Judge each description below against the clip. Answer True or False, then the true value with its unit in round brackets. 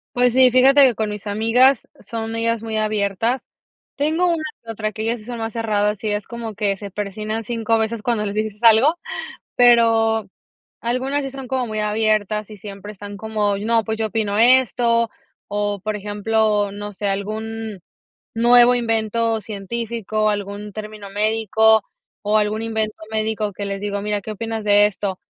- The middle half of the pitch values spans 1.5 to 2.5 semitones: True (1.8 semitones)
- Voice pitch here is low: False (220 Hz)